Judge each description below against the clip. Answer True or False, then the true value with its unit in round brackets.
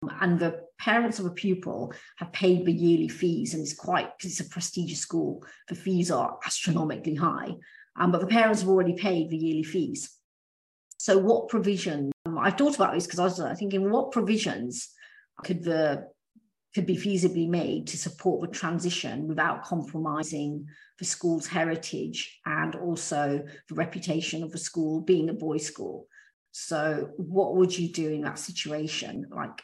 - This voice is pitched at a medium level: True (175 Hz)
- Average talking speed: True (170 wpm)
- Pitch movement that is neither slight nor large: True (3.2 semitones)